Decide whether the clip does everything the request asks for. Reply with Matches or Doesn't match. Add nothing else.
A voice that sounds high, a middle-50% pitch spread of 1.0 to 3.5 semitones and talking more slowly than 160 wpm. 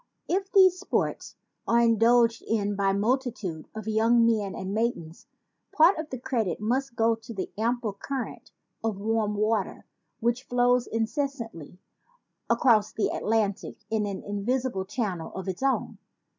Matches